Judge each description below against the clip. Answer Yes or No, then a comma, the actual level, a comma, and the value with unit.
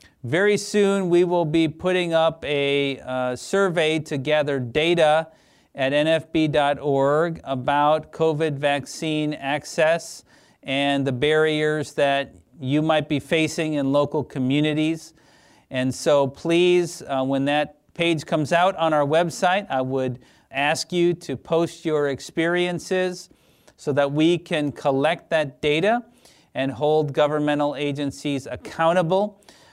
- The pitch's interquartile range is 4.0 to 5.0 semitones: No, average, 2.7 semitones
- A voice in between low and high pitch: Yes, medium, 150 Hz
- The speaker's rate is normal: No, slow, 125 wpm